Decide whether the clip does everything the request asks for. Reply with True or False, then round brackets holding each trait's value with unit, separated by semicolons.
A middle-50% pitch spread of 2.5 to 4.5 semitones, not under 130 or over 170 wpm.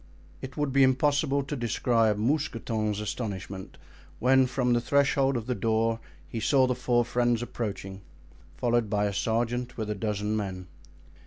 True (3.3 semitones; 155 wpm)